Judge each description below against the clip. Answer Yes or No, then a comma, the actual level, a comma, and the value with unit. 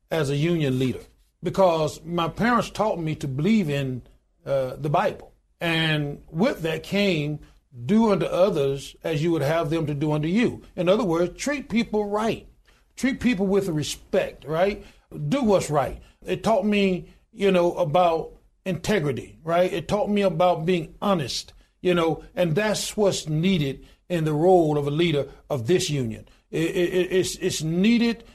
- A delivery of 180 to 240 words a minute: No, average, 165 wpm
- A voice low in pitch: No, medium, 175 Hz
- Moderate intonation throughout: Yes, average, 4.2 semitones